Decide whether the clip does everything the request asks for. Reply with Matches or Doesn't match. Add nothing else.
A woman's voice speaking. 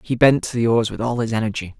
Doesn't match